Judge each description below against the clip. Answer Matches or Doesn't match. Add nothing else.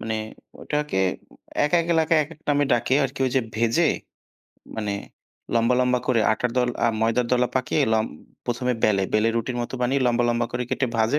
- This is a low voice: Matches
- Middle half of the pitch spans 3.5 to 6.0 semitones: Doesn't match